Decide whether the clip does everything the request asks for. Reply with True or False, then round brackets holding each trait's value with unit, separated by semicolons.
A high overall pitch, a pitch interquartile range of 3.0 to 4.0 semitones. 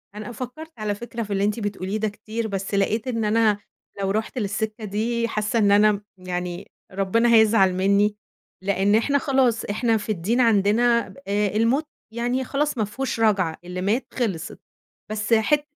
False (215 Hz; 2.6 semitones)